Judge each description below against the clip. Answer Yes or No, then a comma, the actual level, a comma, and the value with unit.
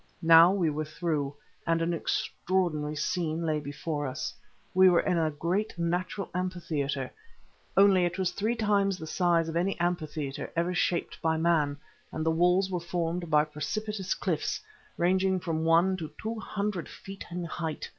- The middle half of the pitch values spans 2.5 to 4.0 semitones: Yes, average, 2.8 semitones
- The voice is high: No, medium, 170 Hz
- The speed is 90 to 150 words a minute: No, average, 165 wpm